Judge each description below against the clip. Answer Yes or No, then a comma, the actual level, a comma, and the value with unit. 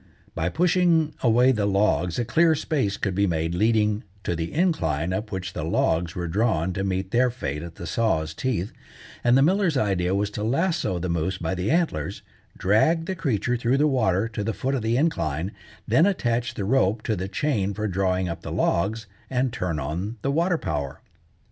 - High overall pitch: No, low, 105 Hz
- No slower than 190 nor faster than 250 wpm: Yes, average, 200 wpm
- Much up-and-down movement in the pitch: Yes, wide, 6.2 semitones